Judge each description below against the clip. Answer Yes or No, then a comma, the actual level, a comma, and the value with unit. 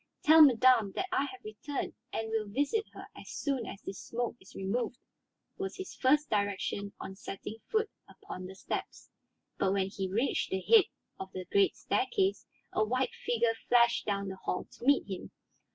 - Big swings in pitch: Yes, wide, 6.8 semitones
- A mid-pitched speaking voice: No, high, 235 Hz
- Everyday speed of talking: Yes, average, 180 wpm